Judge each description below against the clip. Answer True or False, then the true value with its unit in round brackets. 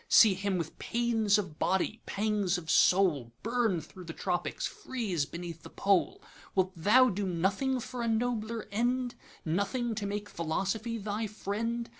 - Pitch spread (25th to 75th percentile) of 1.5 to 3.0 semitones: False (4.1 semitones)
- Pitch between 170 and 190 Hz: False (205 Hz)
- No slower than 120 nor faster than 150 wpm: True (140 wpm)